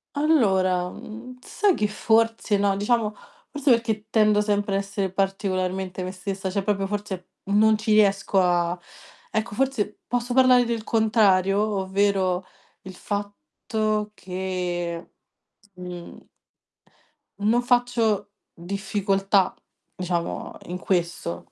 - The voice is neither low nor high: No, high, 200 Hz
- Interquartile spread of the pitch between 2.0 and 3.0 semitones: Yes, average, 2.7 semitones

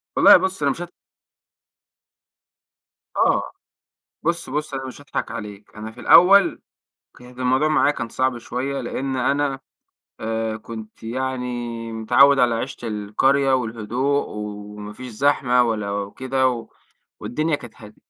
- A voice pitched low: Yes, low, 125 Hz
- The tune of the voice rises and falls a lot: No, average, 3.6 semitones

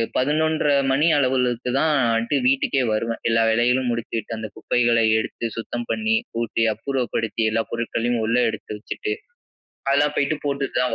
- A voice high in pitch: No, low, 120 Hz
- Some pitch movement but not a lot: Yes, average, 3.3 semitones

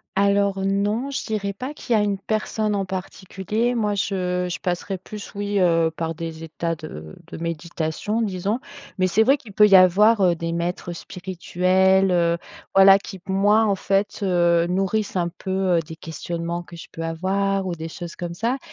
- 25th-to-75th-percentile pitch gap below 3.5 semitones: Yes, average, 2.9 semitones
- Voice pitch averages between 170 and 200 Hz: Yes, high, 190 Hz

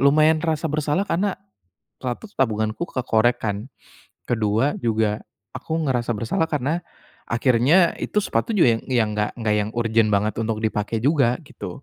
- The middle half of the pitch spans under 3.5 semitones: No, wide, 5.4 semitones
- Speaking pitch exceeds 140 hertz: No, low, 120 Hz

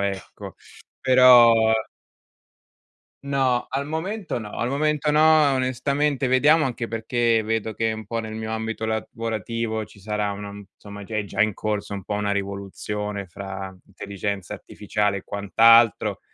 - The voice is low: Yes, low, 110 Hz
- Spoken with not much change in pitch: No, average, 3.9 semitones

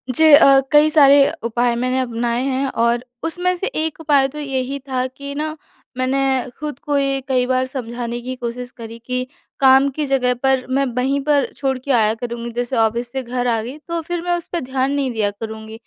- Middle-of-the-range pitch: No, very high, 260 Hz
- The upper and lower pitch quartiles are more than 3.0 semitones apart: No, average, 2.7 semitones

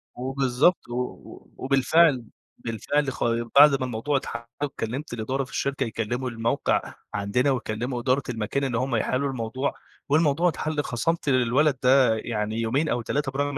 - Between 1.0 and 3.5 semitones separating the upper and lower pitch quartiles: Yes, average, 3.1 semitones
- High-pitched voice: No, low, 130 Hz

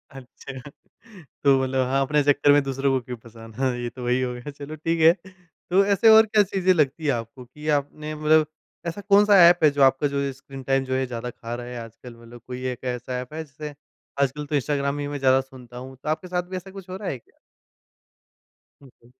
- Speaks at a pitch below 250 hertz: Yes, medium, 140 Hz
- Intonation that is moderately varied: Yes, average, 3.4 semitones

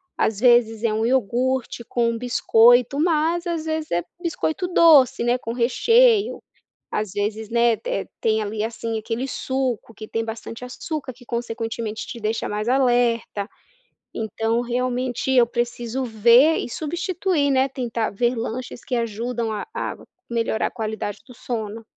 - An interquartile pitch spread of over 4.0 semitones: No, average, 2.7 semitones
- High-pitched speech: Yes, high, 240 Hz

